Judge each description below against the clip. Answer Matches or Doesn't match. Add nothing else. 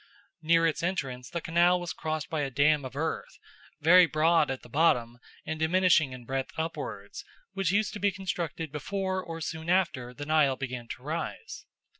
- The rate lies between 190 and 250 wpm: Doesn't match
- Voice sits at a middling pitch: Matches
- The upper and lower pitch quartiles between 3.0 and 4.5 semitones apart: Matches